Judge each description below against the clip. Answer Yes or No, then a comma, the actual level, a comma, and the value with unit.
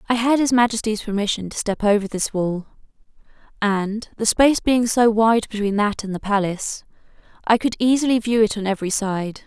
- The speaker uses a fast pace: No, average, 185 wpm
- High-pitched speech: Yes, high, 215 Hz